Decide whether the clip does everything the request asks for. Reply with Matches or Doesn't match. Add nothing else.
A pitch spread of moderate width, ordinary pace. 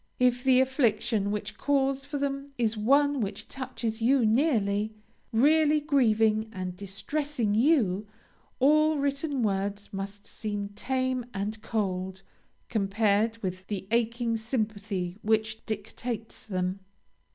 Doesn't match